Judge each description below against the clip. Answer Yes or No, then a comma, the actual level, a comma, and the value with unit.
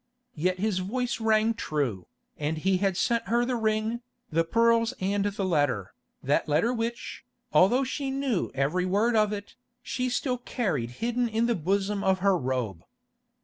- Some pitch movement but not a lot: No, wide, 5.8 semitones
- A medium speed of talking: Yes, average, 165 wpm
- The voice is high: Yes, high, 205 Hz